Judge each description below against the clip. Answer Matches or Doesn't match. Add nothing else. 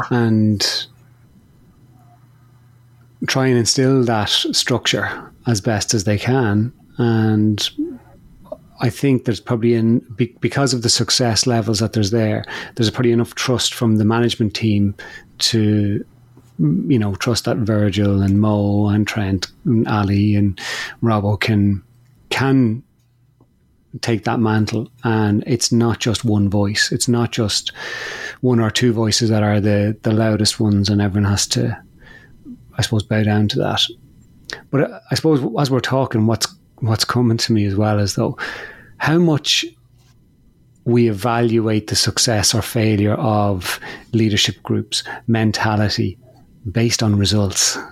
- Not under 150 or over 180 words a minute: Doesn't match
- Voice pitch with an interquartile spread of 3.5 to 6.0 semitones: Doesn't match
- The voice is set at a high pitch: Doesn't match